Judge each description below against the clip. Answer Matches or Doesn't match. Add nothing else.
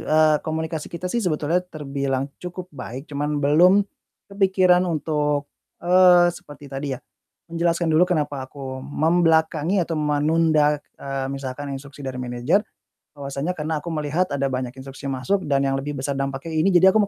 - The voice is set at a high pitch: Doesn't match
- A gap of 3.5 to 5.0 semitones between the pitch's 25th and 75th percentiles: Matches